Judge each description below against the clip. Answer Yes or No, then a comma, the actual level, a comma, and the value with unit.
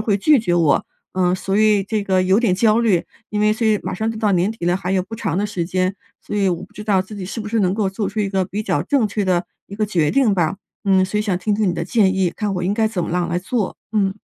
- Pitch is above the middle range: Yes, high, 195 Hz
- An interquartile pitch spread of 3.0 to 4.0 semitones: No, narrow, 2.6 semitones